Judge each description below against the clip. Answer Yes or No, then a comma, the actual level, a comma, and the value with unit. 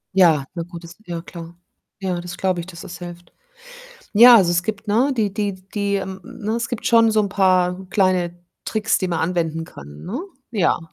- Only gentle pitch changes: No, average, 3.3 semitones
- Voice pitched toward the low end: No, medium, 185 Hz